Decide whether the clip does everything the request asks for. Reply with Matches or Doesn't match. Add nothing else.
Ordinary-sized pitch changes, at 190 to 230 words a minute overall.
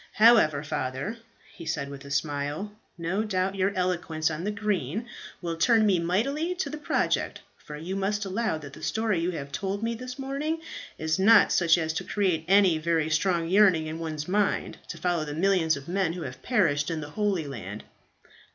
Matches